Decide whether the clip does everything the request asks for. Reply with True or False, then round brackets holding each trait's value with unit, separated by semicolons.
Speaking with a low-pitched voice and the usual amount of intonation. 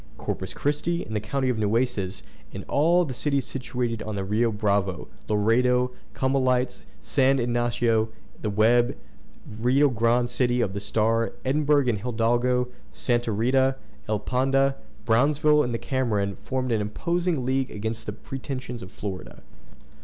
True (120 Hz; 3.2 semitones)